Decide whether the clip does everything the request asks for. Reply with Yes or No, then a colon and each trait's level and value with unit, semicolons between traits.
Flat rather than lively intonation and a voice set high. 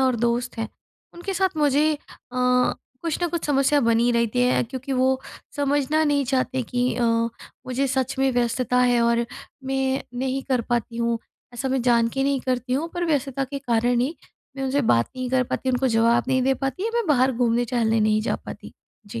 Yes: narrow, 2.3 semitones; very high, 255 Hz